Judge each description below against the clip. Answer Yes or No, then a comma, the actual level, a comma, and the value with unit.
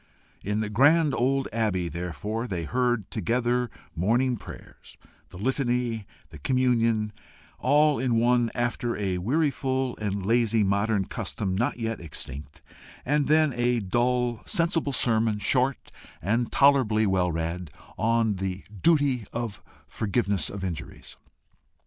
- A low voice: Yes, low, 115 Hz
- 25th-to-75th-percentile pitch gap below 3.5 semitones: No, average, 4.1 semitones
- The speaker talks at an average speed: No, slow, 130 wpm